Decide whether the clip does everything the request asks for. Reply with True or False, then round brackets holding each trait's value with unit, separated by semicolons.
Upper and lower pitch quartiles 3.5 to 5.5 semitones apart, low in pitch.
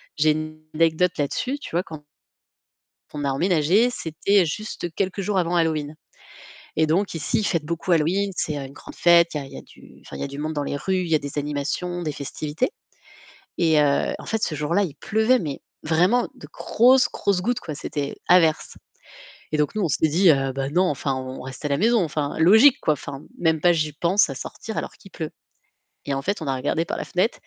False (4.2 semitones; 160 Hz)